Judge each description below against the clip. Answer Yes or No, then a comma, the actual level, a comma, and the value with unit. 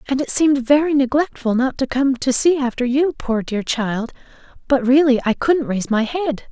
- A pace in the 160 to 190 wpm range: No, fast, 205 wpm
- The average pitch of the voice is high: Yes, very high, 265 Hz